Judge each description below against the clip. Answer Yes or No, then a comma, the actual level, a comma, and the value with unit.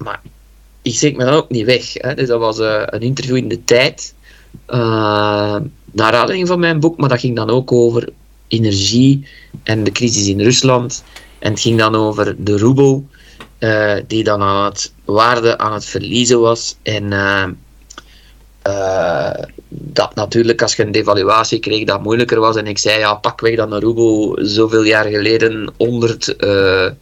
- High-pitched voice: No, low, 115 Hz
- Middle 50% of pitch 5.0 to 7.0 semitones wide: No, average, 3.1 semitones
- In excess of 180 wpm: No, average, 175 wpm